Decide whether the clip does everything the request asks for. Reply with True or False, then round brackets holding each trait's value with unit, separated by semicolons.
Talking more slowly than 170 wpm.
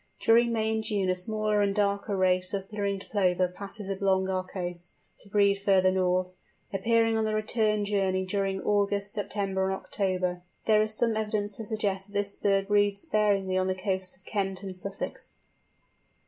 False (175 wpm)